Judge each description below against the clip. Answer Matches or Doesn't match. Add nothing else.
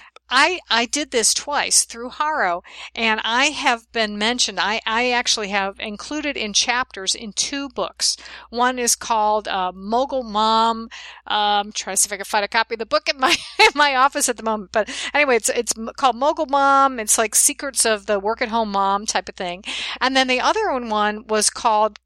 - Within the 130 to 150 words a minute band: Doesn't match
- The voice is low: Doesn't match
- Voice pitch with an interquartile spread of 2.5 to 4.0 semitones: Matches